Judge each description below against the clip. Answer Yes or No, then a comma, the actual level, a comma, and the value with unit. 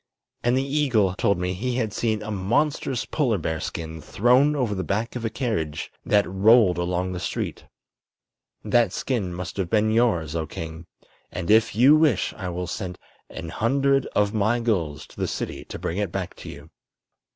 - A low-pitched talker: Yes, low, 105 Hz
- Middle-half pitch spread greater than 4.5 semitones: Yes, average, 5.2 semitones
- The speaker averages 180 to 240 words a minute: Yes, average, 185 wpm